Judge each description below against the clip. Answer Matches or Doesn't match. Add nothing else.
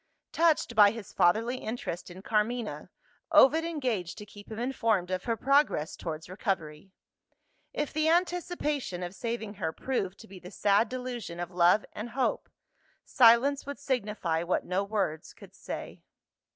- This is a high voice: Matches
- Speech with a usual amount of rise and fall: Doesn't match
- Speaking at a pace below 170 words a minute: Matches